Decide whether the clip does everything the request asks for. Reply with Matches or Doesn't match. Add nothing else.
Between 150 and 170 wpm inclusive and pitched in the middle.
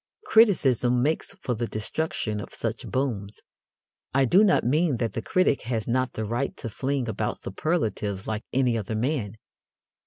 Doesn't match